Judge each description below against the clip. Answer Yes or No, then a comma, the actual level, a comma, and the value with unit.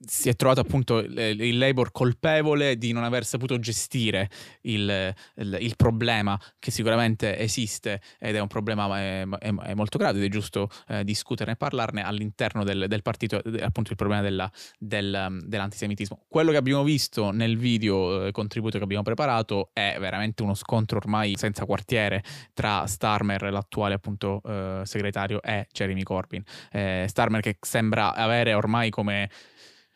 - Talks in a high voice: No, low, 105 Hz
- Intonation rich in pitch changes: No, average, 2.7 semitones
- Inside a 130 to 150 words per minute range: No, average, 160 wpm